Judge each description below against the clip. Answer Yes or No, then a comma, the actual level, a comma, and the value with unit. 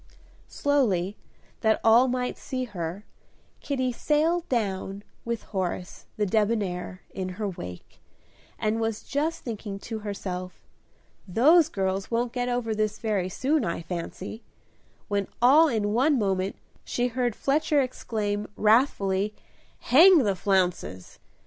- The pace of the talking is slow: Yes, slow, 125 wpm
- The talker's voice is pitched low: No, high, 215 Hz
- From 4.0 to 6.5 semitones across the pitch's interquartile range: Yes, average, 4.6 semitones